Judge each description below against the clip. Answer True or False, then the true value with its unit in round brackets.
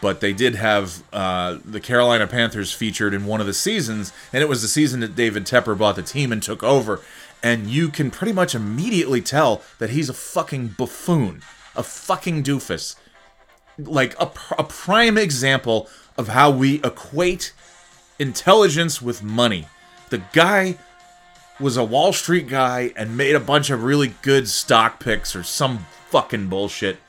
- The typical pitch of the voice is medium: False (130 Hz)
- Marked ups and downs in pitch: True (5.8 semitones)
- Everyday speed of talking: True (170 wpm)